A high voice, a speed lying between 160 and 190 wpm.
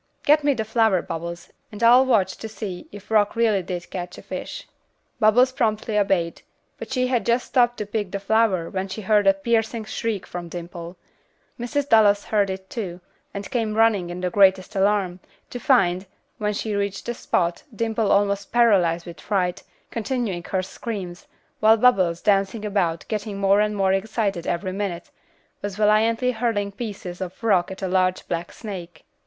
Yes: high, 205 Hz; average, 175 wpm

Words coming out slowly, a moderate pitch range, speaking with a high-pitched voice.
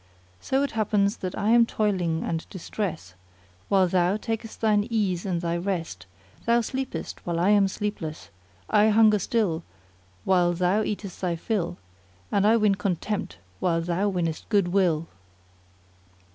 No: average, 145 wpm; average, 3.5 semitones; high, 195 Hz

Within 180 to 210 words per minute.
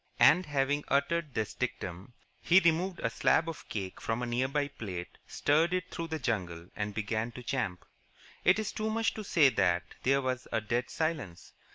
Yes: average, 190 wpm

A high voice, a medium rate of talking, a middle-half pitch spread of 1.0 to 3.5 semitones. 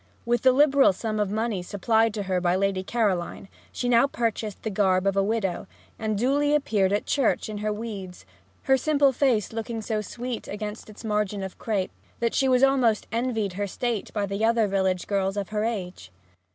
Yes: high, 215 Hz; average, 195 wpm; average, 3.1 semitones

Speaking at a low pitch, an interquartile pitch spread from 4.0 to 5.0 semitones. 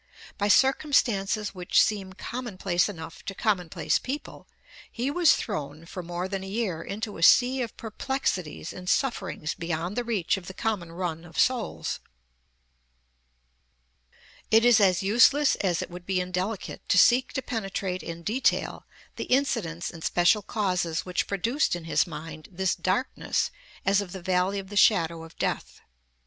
No: high, 190 Hz; average, 4.4 semitones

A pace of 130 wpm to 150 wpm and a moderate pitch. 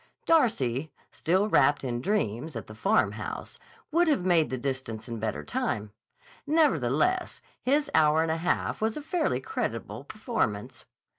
Yes: average, 145 wpm; medium, 160 Hz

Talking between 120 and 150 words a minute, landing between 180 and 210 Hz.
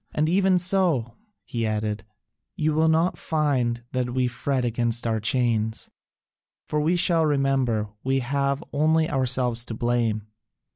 No: average, 140 wpm; low, 130 Hz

